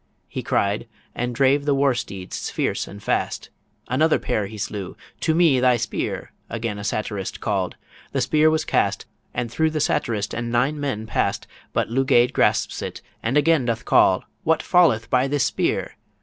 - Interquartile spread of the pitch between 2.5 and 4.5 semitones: No, average, 4.9 semitones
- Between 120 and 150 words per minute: No, average, 175 wpm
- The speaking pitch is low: Yes, low, 125 Hz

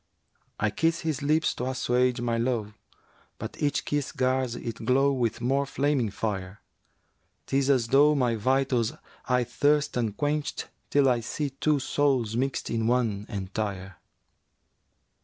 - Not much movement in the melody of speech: No, average, 3.4 semitones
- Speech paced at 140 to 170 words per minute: Yes, average, 145 wpm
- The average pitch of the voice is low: Yes, low, 125 Hz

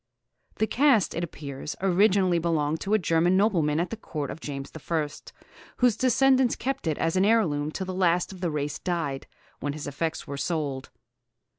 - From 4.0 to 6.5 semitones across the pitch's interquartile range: Yes, average, 5.0 semitones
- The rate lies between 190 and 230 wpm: No, average, 180 wpm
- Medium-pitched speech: Yes, medium, 170 Hz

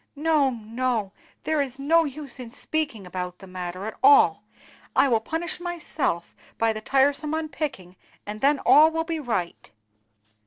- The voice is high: Yes, very high, 270 Hz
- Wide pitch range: Yes, wide, 6.6 semitones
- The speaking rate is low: No, average, 155 wpm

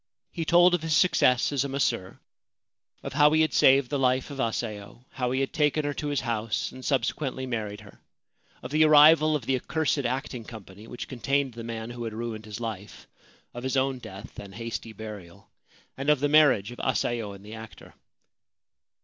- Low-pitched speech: Yes, low, 125 Hz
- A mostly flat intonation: No, average, 4.3 semitones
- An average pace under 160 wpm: No, average, 195 wpm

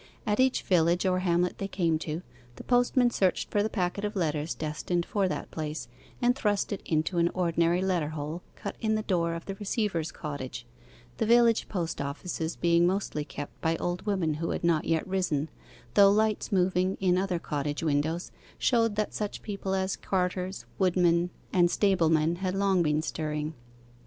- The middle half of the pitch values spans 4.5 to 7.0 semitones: No, average, 3.4 semitones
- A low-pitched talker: No, medium, 180 Hz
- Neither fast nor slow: Yes, average, 175 wpm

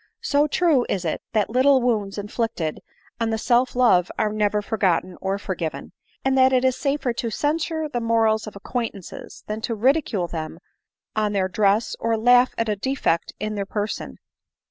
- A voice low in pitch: No, high, 220 Hz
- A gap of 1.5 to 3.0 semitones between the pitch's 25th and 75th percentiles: No, average, 4.0 semitones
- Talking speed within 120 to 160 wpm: No, average, 180 wpm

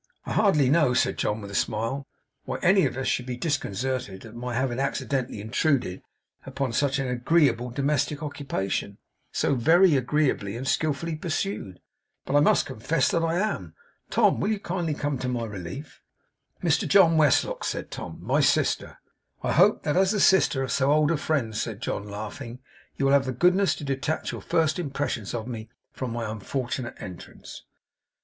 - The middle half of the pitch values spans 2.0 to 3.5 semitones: No, average, 5.0 semitones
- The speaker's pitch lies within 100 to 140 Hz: Yes, low, 135 Hz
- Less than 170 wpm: No, average, 180 wpm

